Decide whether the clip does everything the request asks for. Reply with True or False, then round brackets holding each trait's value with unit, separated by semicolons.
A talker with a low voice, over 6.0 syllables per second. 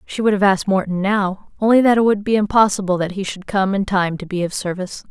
False (195 Hz; 6.2 syllables/s)